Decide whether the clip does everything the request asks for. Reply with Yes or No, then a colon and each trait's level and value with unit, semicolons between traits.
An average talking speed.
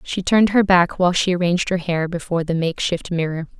No: fast, 215 wpm